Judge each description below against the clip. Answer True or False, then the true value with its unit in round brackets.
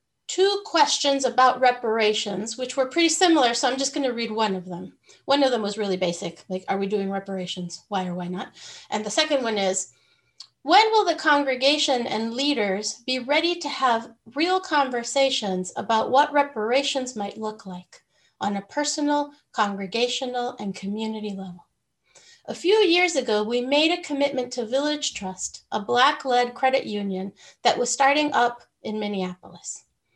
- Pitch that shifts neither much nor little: False (5.7 semitones)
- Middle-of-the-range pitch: False (245 Hz)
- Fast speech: False (165 wpm)